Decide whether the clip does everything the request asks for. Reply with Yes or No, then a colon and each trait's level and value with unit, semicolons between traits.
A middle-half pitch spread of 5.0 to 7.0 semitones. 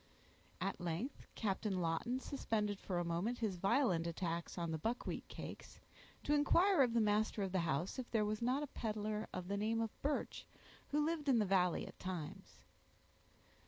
Yes: average, 5.3 semitones